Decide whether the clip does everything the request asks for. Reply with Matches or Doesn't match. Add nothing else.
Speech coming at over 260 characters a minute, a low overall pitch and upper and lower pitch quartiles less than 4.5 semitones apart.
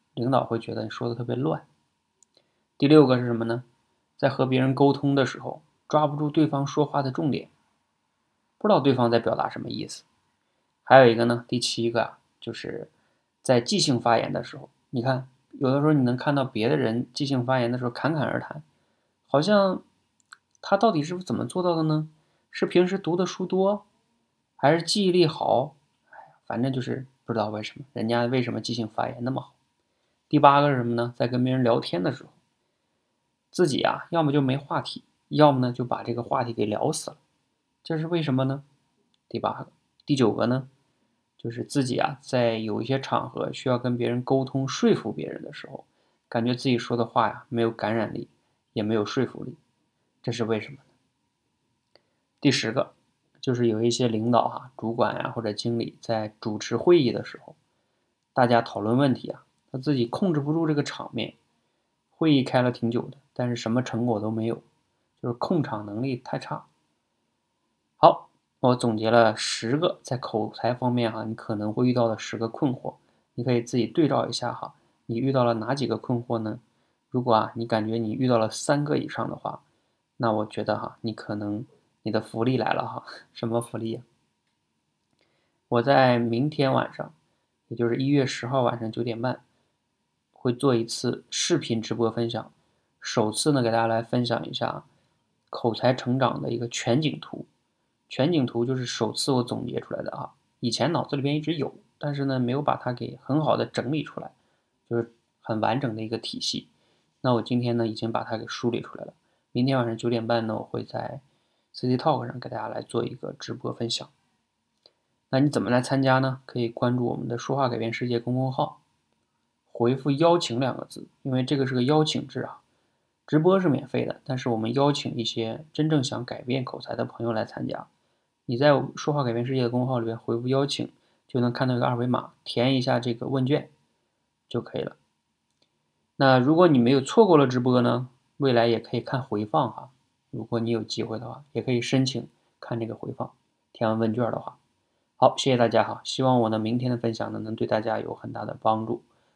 Matches